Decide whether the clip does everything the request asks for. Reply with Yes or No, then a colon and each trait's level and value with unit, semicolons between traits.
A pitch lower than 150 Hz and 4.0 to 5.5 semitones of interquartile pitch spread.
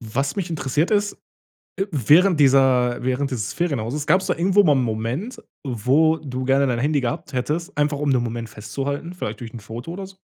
Yes: medium, 140 Hz; average, 4.9 semitones